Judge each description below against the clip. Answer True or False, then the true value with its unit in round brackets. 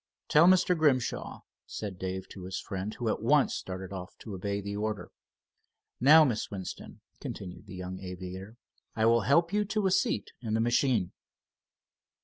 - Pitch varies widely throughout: True (6.6 semitones)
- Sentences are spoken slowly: False (165 wpm)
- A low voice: True (105 Hz)